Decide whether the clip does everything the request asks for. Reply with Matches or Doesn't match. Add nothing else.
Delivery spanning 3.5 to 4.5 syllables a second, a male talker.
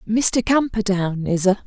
Doesn't match